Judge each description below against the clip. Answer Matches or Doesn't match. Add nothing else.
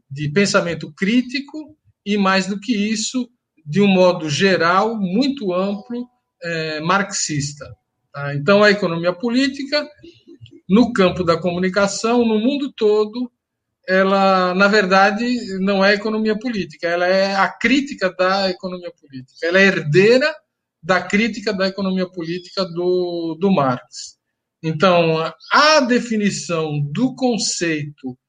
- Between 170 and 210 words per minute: Doesn't match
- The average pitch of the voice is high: Matches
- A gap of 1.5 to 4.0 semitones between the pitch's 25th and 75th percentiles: Doesn't match